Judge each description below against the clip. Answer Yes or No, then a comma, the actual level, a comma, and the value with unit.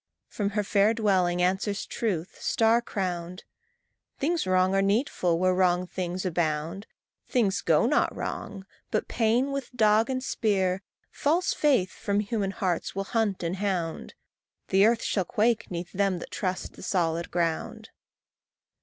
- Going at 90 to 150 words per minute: Yes, average, 145 wpm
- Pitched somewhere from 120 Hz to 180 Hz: No, high, 195 Hz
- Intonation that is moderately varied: Yes, average, 3.5 semitones